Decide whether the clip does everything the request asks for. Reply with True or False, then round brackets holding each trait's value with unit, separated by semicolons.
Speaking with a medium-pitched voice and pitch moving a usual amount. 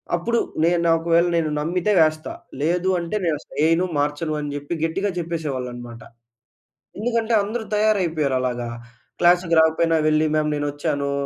True (165 Hz; 3.1 semitones)